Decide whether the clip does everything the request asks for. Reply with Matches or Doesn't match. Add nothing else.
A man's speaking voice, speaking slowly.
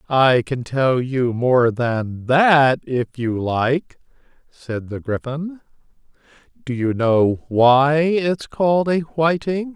Matches